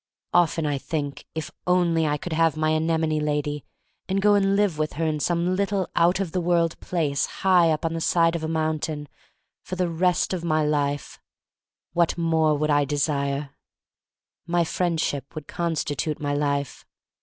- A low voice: No, medium, 160 Hz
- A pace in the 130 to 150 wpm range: No, average, 180 wpm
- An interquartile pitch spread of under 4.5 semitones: Yes, narrow, 2.6 semitones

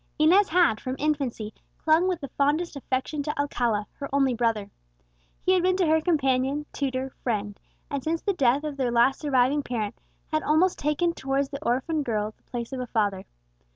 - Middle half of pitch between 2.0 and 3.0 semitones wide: No, average, 4.1 semitones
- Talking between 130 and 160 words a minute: No, average, 190 wpm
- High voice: Yes, very high, 275 Hz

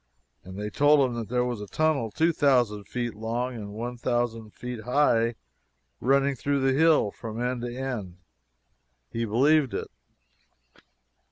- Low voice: Yes, low, 120 Hz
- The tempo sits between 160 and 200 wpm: No, average, 140 wpm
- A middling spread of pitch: Yes, average, 3.2 semitones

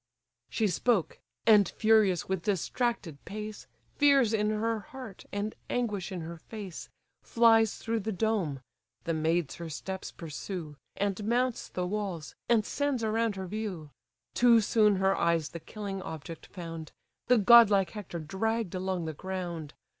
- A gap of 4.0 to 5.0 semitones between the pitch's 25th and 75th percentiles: Yes, average, 4.6 semitones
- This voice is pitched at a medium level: No, high, 200 Hz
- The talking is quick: No, average, 145 wpm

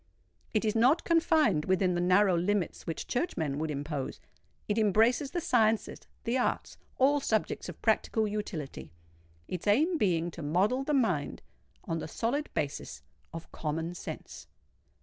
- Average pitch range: No, wide, 7.0 semitones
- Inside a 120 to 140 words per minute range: Yes, slow, 135 wpm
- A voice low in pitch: No, high, 195 Hz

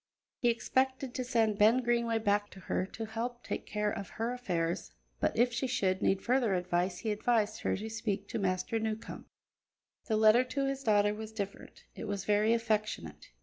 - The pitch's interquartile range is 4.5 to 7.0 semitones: No, average, 2.8 semitones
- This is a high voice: Yes, high, 220 Hz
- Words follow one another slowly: No, average, 190 wpm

